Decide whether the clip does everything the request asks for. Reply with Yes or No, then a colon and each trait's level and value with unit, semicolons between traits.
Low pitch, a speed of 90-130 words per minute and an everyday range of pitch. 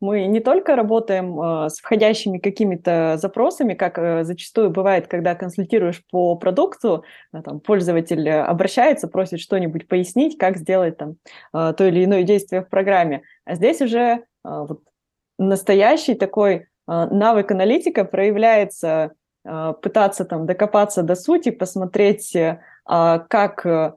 No: high, 190 Hz; average, 115 wpm; average, 3.3 semitones